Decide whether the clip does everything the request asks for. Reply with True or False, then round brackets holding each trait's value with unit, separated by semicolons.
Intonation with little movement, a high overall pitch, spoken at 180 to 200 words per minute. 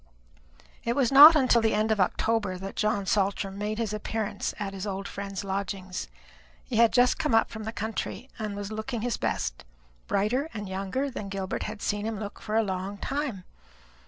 True (2.3 semitones; 210 Hz; 190 wpm)